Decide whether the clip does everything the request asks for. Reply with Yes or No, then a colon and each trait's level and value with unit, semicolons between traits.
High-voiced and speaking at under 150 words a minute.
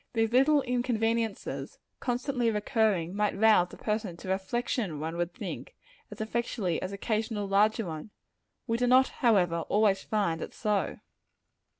Yes: high, 215 Hz; average, 140 wpm